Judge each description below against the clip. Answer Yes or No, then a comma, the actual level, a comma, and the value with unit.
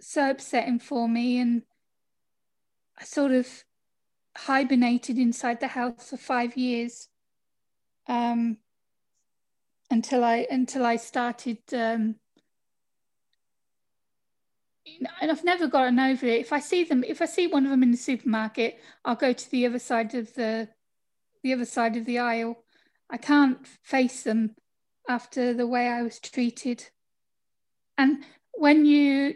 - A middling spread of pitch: No, narrow, 2.3 semitones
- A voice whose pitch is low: No, high, 245 Hz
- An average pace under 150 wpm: Yes, average, 140 wpm